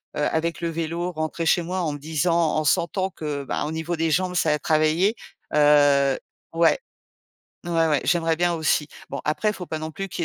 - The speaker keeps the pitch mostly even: Yes, narrow, 2.1 semitones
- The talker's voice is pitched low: No, medium, 160 Hz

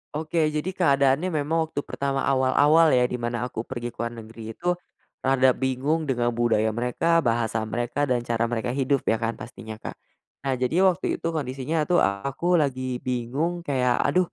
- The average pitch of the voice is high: No, low, 130 Hz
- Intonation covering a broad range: No, average, 3.4 semitones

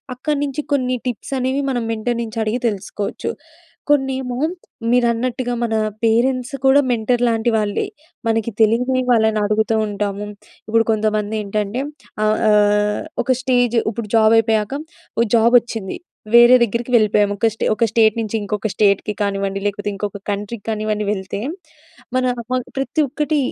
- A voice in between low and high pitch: No, high, 225 Hz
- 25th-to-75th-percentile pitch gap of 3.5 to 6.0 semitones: No, average, 2.8 semitones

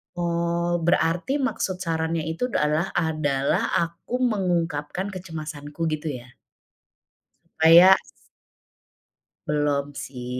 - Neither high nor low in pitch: Yes, medium, 165 Hz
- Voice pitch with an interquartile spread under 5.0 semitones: Yes, average, 2.9 semitones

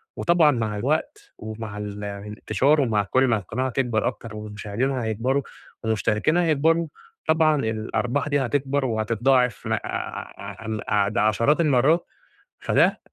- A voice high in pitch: No, low, 120 Hz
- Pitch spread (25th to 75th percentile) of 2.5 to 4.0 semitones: No, average, 4.7 semitones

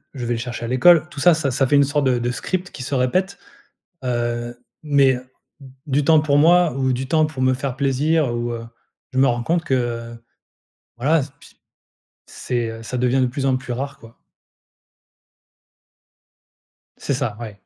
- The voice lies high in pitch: No, low, 130 Hz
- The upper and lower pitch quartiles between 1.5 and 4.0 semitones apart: Yes, average, 3.4 semitones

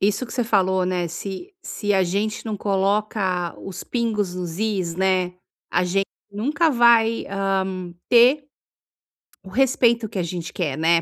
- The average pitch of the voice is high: Yes, high, 195 Hz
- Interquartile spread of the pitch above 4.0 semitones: No, average, 3.6 semitones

